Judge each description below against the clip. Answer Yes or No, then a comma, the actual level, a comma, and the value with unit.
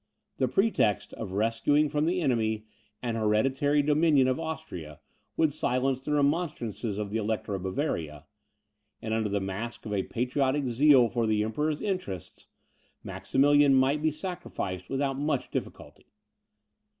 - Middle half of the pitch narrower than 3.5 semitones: No, average, 5.3 semitones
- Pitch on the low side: Yes, low, 130 Hz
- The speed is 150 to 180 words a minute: No, average, 140 wpm